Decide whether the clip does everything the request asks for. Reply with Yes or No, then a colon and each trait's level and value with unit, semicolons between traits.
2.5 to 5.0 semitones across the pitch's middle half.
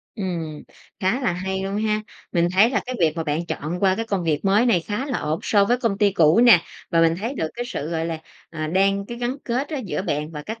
No: wide, 5.4 semitones